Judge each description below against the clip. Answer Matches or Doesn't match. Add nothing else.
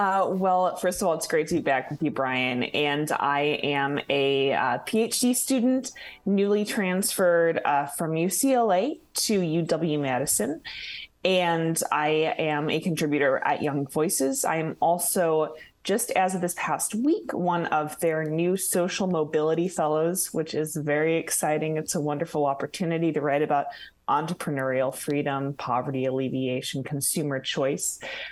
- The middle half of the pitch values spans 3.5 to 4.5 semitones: Matches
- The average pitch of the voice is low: Doesn't match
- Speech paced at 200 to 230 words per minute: Doesn't match